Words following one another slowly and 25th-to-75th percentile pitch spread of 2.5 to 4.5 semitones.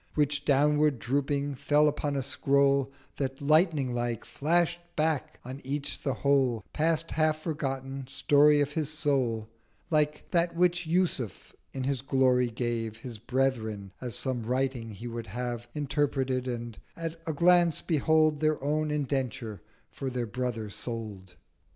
No: average, 145 wpm; average, 3.7 semitones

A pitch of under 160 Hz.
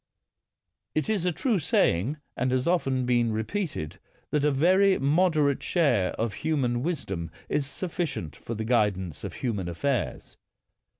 Yes: low, 135 Hz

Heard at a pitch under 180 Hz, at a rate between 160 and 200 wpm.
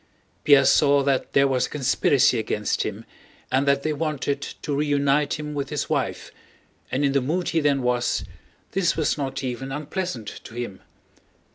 Yes: medium, 140 Hz; average, 170 wpm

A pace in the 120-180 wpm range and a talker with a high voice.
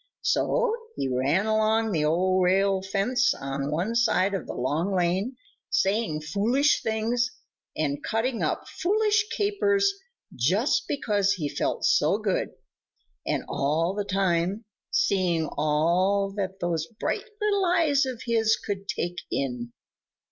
Yes: slow, 135 wpm; high, 195 Hz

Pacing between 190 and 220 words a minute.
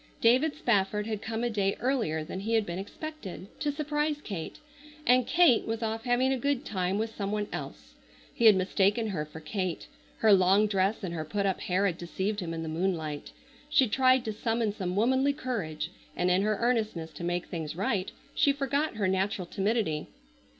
Yes: average, 195 wpm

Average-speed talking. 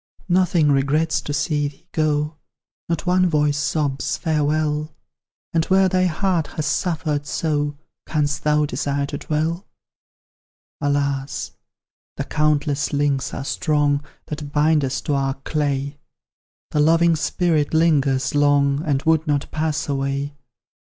No: slow, 130 wpm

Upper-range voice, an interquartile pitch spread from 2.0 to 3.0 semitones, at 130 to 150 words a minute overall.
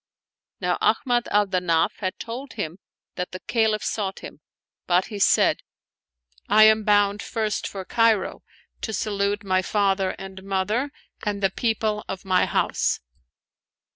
Yes: high, 200 Hz; narrow, 2.4 semitones; average, 145 wpm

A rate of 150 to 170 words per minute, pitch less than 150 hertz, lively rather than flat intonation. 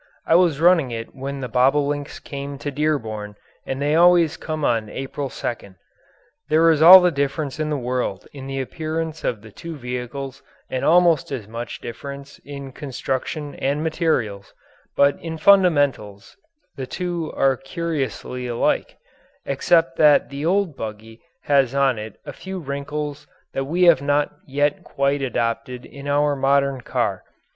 No: average, 155 wpm; medium, 140 Hz; average, 3.4 semitones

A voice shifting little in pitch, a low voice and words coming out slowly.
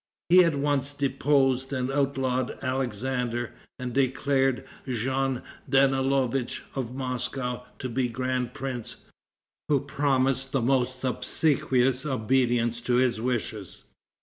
Yes: narrow, 1.5 semitones; low, 130 Hz; slow, 110 wpm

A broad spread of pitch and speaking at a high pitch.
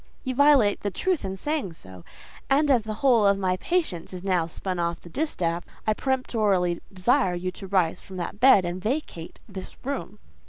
Yes: wide, 6.6 semitones; high, 195 Hz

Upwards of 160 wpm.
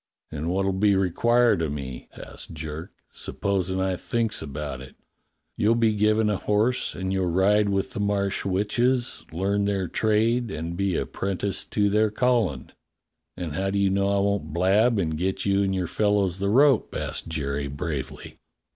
Yes: average, 170 wpm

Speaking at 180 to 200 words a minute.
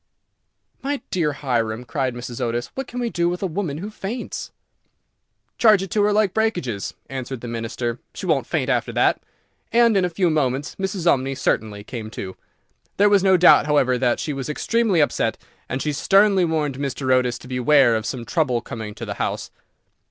Yes: average, 190 wpm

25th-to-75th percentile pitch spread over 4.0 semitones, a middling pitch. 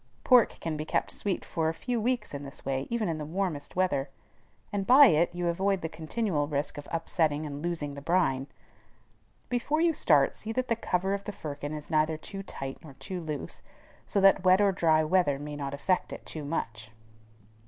Yes: average, 5.0 semitones; medium, 165 Hz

